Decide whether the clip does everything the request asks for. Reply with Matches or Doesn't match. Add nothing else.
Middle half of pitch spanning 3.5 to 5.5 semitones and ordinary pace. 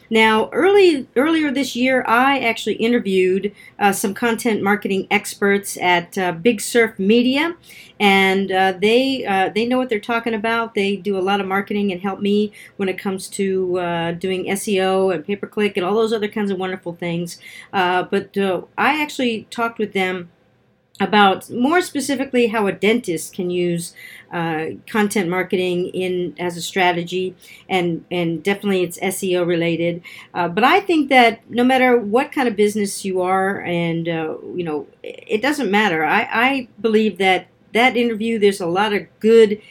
Matches